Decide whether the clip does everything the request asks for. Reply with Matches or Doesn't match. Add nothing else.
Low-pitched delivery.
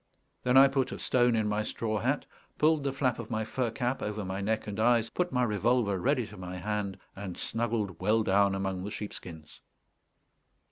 Matches